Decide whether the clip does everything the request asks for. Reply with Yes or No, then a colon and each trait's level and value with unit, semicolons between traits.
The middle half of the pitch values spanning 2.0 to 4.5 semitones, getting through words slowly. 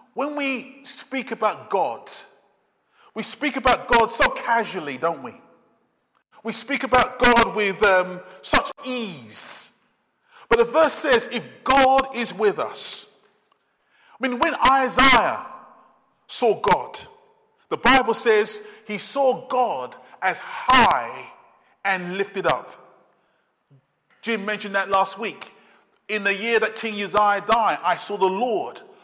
Yes: average, 4.2 semitones; slow, 130 wpm